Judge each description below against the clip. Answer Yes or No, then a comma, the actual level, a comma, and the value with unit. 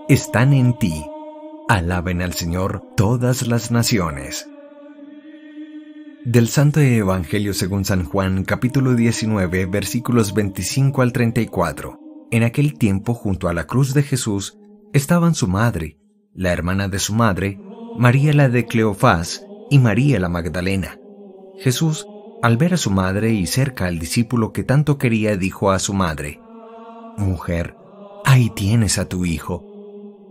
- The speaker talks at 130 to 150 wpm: Yes, slow, 135 wpm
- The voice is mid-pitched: No, low, 120 Hz